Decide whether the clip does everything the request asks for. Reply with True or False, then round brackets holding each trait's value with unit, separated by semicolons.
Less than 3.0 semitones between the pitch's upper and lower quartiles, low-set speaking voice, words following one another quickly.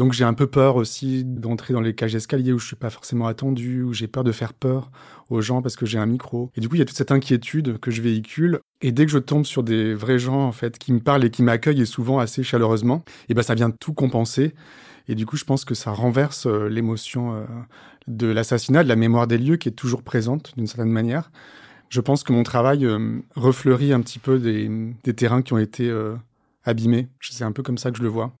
True (2.5 semitones; 120 Hz; 260 wpm)